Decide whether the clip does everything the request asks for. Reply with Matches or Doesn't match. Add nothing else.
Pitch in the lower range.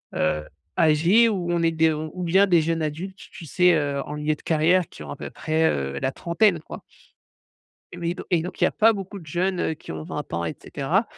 Doesn't match